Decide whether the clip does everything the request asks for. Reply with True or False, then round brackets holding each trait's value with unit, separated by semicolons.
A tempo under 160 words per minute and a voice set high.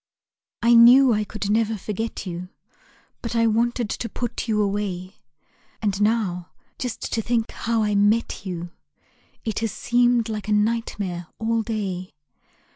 True (145 wpm; 220 Hz)